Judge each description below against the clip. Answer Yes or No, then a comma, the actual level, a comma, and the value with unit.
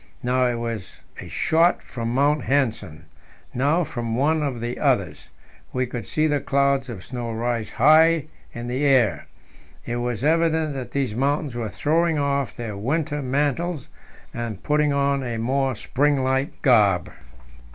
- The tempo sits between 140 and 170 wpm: Yes, average, 155 wpm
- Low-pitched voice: Yes, low, 130 Hz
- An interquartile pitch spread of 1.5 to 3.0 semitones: No, average, 3.7 semitones